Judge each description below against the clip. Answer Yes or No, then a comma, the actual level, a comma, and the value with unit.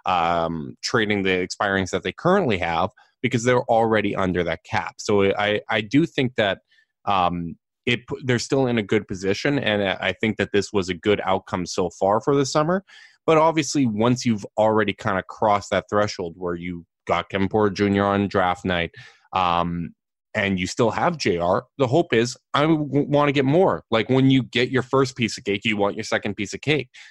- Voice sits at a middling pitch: No, low, 110 Hz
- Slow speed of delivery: No, average, 200 wpm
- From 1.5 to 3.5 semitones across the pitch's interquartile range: No, wide, 5.5 semitones